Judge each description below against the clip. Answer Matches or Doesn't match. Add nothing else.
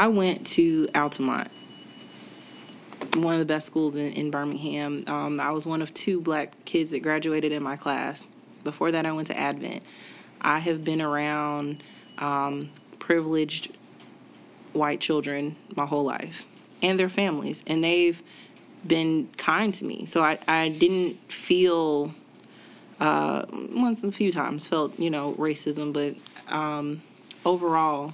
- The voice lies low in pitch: Doesn't match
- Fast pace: Doesn't match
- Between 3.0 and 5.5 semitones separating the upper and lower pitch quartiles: Doesn't match